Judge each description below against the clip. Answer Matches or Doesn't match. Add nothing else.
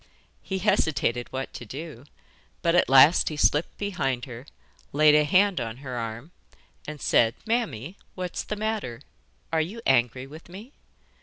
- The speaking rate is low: Doesn't match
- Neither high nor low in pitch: Matches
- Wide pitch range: Matches